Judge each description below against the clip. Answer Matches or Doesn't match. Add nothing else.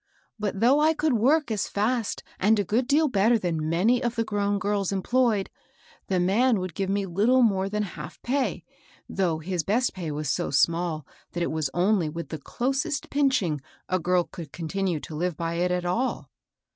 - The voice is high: Matches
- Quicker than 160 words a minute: Matches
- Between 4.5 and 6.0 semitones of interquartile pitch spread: Matches